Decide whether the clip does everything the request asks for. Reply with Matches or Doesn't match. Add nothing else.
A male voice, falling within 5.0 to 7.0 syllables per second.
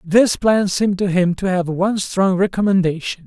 Matches